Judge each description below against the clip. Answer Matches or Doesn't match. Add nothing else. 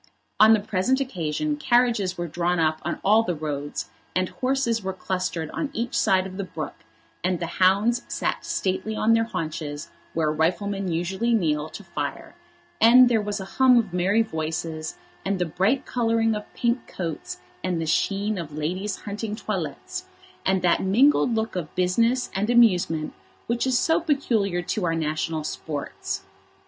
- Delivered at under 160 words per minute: Doesn't match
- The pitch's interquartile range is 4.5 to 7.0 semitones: Matches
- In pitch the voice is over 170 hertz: Matches